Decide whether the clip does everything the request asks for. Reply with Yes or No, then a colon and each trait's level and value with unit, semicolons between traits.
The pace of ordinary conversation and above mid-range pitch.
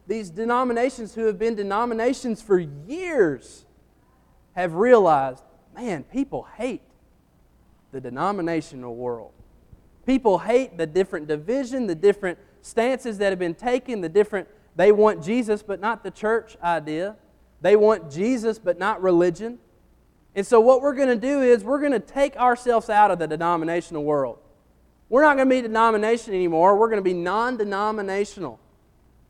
Yes: average, 150 wpm; high, 210 Hz